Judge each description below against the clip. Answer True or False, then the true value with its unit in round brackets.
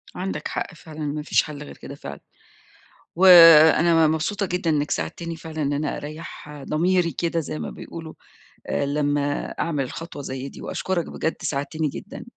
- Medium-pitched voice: True (155 Hz)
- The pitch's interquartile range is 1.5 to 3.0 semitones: True (2.5 semitones)